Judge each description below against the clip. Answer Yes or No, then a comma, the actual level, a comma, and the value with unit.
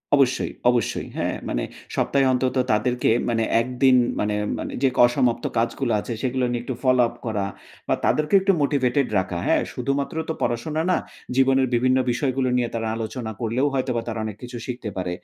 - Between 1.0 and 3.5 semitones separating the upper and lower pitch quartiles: Yes, narrow, 2.5 semitones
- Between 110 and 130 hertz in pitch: Yes, low, 125 Hz